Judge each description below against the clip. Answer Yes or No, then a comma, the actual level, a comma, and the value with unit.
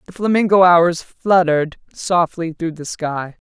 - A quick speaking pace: No, average, 140 wpm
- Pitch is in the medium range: Yes, medium, 170 Hz